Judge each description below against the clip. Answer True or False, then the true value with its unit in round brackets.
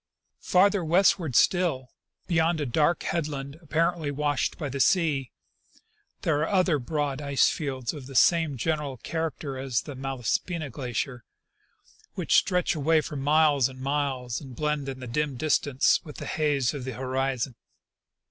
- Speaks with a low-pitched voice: False (145 Hz)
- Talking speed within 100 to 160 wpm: True (150 wpm)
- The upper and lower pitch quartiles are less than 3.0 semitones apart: False (3.3 semitones)